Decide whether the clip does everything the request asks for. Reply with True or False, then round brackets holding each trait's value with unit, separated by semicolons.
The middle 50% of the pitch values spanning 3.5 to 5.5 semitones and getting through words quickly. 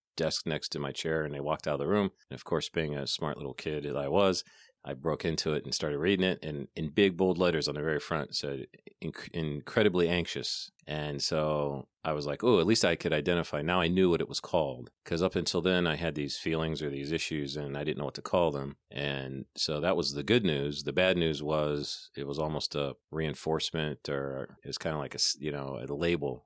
False (2.8 semitones; 245 wpm)